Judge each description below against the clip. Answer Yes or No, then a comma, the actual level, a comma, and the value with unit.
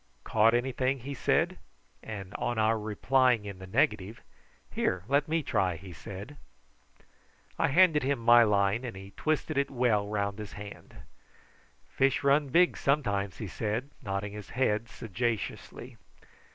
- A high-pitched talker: No, low, 110 Hz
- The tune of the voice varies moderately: Yes, average, 4.8 semitones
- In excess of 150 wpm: No, average, 145 wpm